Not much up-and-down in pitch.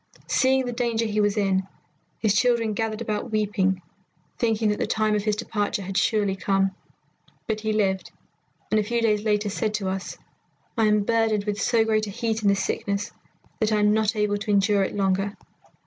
Yes: narrow, 1.7 semitones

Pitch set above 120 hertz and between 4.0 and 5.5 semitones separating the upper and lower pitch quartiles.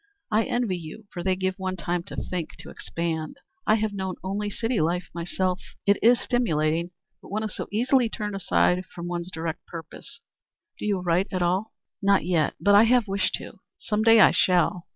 No: high, 190 Hz; average, 3.6 semitones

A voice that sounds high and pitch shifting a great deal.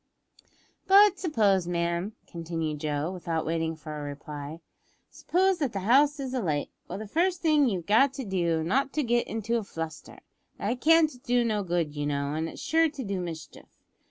Yes: high, 195 Hz; wide, 8.8 semitones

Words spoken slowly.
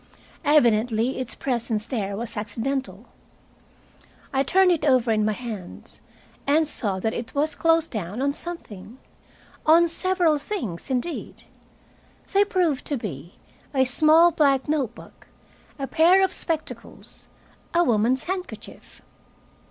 Yes: slow, 130 wpm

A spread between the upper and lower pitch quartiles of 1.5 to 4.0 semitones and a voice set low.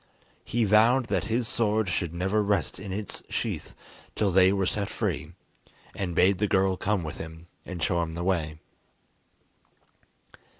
Yes: average, 3.4 semitones; very low, 95 Hz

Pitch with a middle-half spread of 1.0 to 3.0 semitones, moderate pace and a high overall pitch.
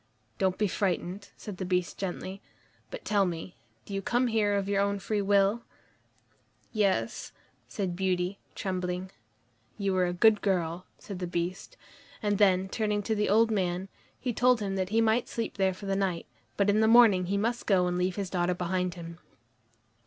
Yes: narrow, 2.5 semitones; average, 185 wpm; high, 195 Hz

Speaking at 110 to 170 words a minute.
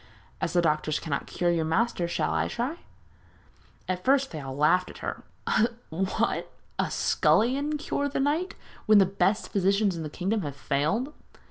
Yes: average, 165 wpm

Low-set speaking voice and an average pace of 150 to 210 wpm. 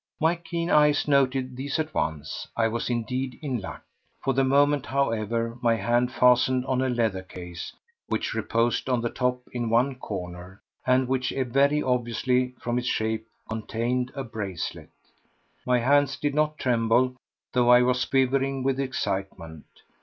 Yes: low, 125 Hz; average, 155 wpm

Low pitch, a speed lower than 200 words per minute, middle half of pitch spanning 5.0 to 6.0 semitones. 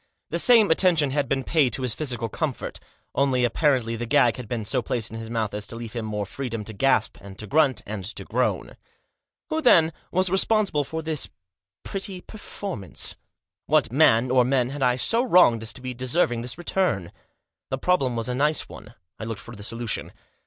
No: low, 125 Hz; fast, 205 wpm; wide, 5.4 semitones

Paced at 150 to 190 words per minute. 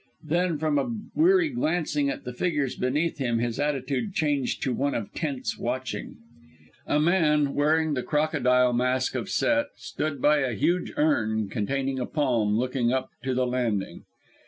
Yes: average, 160 wpm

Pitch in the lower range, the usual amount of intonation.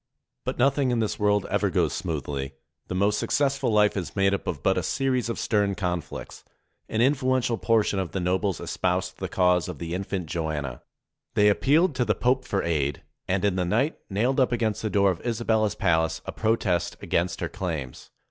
Yes: low, 100 Hz; average, 4.6 semitones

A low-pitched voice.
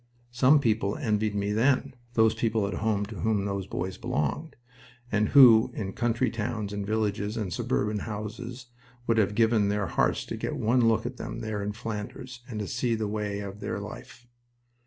Yes: low, 110 Hz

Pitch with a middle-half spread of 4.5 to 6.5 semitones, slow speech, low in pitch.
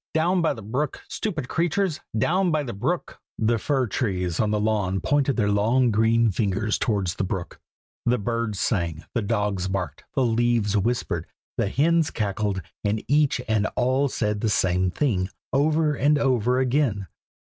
No: average, 5.1 semitones; average, 165 wpm; low, 115 Hz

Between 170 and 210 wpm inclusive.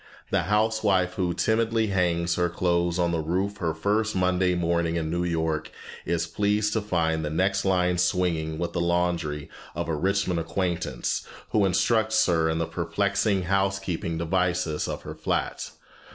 No: average, 160 wpm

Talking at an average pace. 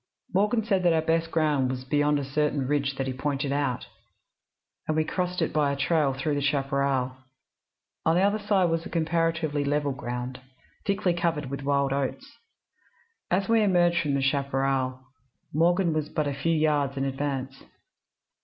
Yes: average, 170 wpm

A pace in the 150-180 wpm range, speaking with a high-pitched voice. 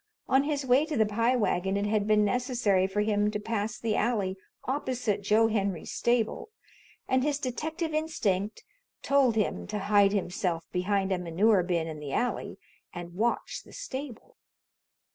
Yes: average, 160 wpm; high, 210 Hz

